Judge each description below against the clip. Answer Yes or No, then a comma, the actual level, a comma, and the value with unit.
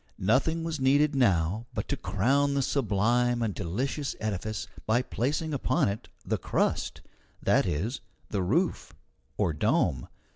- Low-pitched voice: Yes, low, 120 Hz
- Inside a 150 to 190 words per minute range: No, average, 140 wpm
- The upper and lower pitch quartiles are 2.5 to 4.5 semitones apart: No, wide, 5.6 semitones